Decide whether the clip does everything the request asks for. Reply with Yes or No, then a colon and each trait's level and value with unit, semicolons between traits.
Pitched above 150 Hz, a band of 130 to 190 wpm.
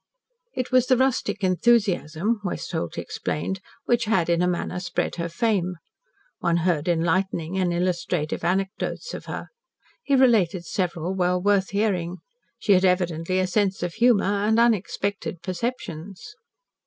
Yes: medium, 185 Hz; average, 140 wpm